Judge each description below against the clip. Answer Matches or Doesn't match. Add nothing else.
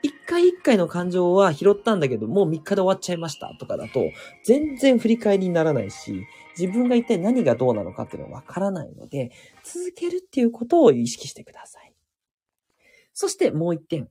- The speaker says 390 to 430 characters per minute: Matches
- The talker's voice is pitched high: Matches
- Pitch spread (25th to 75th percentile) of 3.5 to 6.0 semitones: Doesn't match